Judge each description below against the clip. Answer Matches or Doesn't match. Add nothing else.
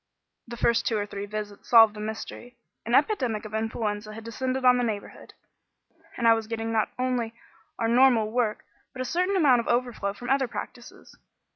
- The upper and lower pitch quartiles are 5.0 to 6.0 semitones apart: Doesn't match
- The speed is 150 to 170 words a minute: Doesn't match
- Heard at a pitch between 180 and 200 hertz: Doesn't match